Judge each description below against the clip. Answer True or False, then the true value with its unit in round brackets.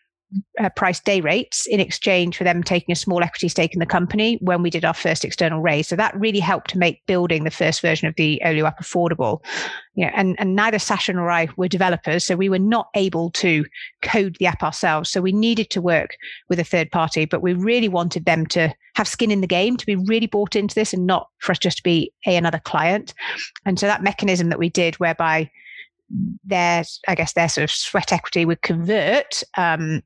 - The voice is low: False (180 Hz)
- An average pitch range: True (3.1 semitones)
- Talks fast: True (230 wpm)